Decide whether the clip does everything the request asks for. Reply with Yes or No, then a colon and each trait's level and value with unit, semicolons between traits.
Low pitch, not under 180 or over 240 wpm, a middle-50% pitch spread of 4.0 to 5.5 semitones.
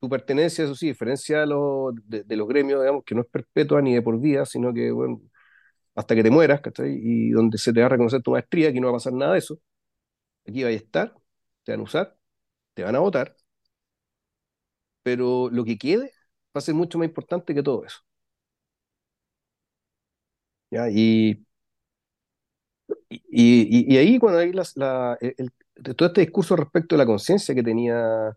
Yes: low, 130 Hz; fast, 190 wpm; average, 5.1 semitones